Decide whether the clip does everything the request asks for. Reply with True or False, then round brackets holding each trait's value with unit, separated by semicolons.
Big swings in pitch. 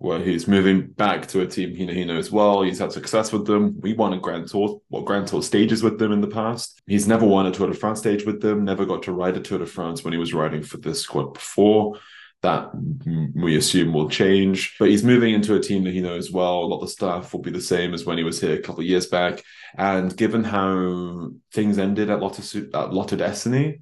False (2.7 semitones)